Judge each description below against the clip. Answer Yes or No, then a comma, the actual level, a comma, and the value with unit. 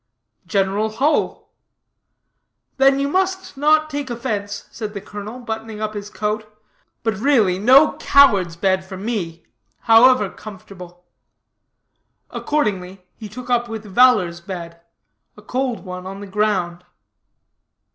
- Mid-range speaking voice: No, high, 215 Hz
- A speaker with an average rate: No, slow, 125 wpm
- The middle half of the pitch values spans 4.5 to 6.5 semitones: Yes, average, 4.9 semitones